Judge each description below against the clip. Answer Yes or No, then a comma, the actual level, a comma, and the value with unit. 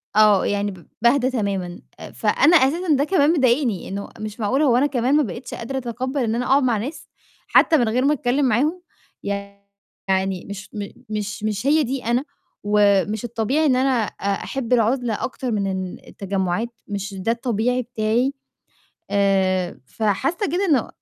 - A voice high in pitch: Yes, high, 230 Hz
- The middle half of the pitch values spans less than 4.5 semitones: No, average, 4.8 semitones